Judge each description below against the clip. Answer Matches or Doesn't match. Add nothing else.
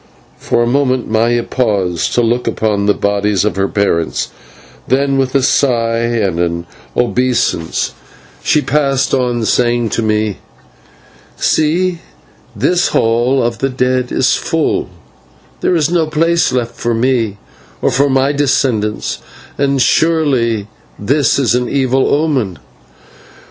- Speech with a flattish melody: Doesn't match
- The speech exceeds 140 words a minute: Doesn't match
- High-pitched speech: Doesn't match